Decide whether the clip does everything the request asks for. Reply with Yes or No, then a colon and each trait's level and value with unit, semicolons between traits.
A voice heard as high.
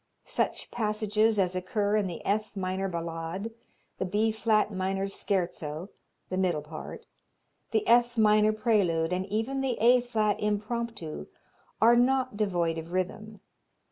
Yes: high, 205 Hz